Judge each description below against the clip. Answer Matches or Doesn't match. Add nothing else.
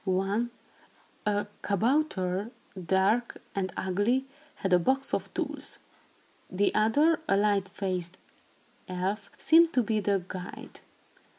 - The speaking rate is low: Matches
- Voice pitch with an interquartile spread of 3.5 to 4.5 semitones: Matches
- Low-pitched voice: Doesn't match